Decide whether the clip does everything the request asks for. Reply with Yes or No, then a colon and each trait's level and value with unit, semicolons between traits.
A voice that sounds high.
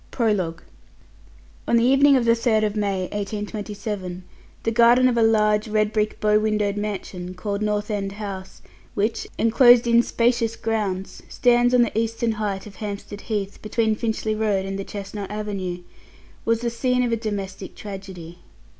Yes: high, 210 Hz